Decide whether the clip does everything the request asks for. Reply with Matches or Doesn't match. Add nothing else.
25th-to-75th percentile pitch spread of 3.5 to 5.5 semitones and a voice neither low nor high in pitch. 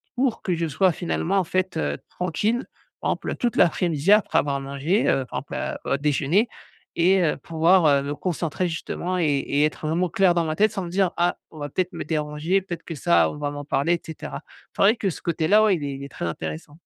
Matches